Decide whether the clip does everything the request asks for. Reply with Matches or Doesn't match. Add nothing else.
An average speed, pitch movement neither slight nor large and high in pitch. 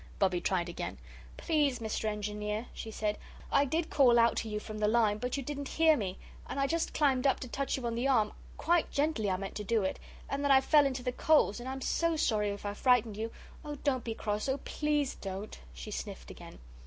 Doesn't match